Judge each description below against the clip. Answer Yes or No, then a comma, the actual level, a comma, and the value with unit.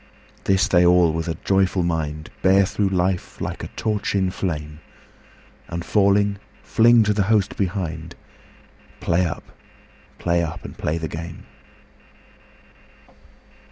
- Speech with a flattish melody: No, average, 3.1 semitones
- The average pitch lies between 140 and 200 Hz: No, very low, 90 Hz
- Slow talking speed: Yes, slow, 130 wpm